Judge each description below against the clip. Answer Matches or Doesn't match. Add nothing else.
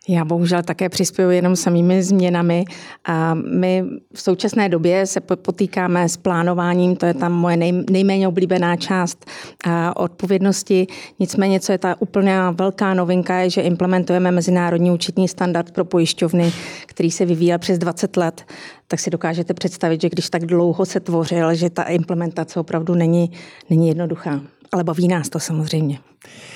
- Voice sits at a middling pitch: Matches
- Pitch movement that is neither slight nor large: Doesn't match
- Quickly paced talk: Doesn't match